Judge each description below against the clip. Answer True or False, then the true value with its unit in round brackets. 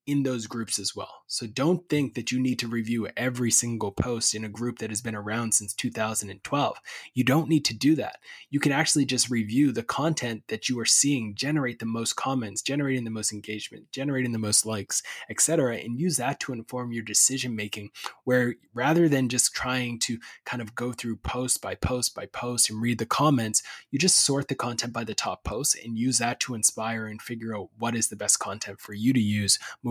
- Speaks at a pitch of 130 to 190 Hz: False (120 Hz)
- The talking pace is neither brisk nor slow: False (220 wpm)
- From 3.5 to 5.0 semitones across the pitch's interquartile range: False (2.8 semitones)